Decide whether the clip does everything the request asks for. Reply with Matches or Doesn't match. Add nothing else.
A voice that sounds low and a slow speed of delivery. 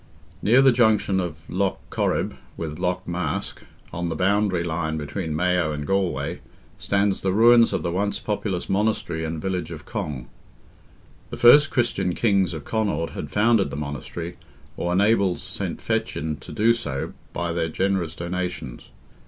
Doesn't match